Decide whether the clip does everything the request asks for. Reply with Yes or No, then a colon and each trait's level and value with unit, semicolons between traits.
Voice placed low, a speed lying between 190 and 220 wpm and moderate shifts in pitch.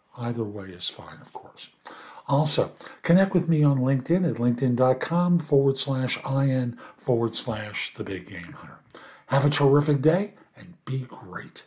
No: low, 130 Hz; average, 155 wpm; average, 4.1 semitones